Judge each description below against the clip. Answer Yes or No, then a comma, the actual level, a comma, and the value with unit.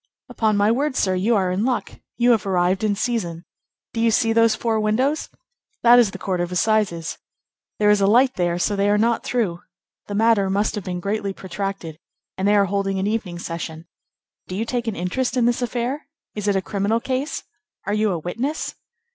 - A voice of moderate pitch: No, high, 210 Hz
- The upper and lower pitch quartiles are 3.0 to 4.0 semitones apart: Yes, average, 3.5 semitones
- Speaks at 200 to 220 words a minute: Yes, fast, 205 wpm